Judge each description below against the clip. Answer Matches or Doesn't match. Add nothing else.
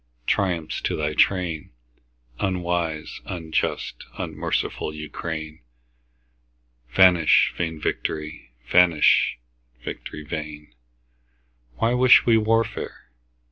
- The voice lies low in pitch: Matches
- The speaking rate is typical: Doesn't match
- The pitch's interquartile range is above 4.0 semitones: Doesn't match